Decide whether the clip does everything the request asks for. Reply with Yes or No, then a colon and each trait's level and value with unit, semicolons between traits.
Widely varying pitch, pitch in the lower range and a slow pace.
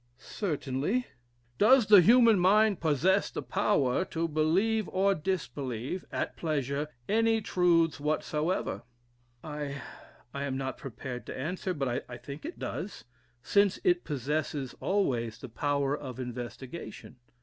No: wide, 6.4 semitones; medium, 155 Hz; slow, 125 wpm